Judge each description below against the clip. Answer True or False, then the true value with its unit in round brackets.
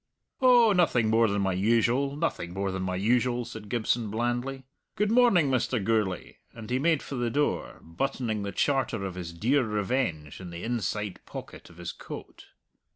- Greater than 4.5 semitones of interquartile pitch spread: True (5.4 semitones)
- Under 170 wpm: False (175 wpm)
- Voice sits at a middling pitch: False (115 Hz)